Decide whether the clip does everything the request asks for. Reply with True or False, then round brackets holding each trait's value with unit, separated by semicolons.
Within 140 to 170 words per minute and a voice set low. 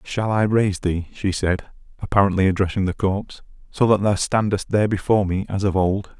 False (195 wpm; 100 Hz)